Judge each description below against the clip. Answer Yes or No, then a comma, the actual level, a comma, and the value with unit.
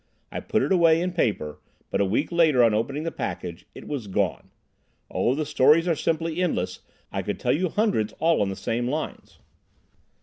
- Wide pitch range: Yes, wide, 7.5 semitones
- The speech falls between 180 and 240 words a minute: Yes, average, 190 wpm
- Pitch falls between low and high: Yes, medium, 150 Hz